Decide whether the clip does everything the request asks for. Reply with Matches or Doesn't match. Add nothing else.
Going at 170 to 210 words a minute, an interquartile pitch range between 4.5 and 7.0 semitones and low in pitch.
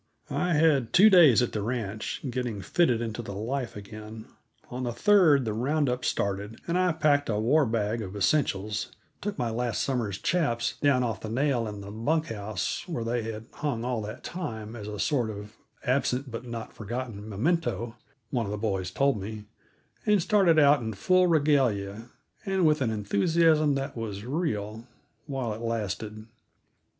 Matches